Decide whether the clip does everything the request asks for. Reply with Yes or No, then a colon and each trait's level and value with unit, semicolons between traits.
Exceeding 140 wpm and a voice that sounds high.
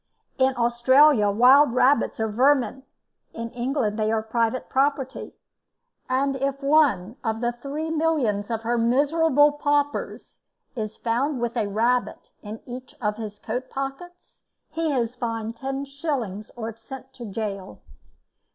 No: slow, 135 wpm; very high, 250 Hz